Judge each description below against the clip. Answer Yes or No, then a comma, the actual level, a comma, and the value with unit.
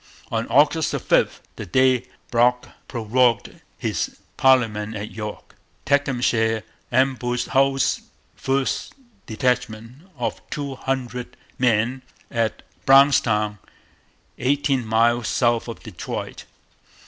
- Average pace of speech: No, slow, 95 wpm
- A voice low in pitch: Yes, low, 125 Hz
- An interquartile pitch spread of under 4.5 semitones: Yes, average, 2.9 semitones